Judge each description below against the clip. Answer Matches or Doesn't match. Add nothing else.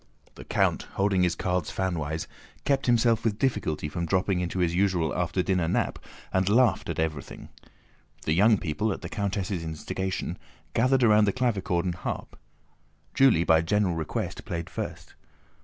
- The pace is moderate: Matches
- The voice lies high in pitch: Doesn't match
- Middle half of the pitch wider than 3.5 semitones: Matches